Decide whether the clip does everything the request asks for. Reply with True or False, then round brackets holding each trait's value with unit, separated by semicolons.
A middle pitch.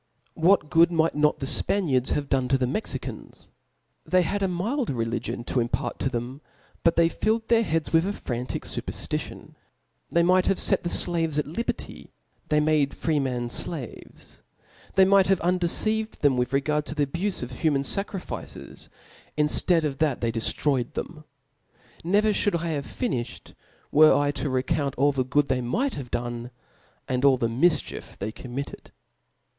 True (150 Hz)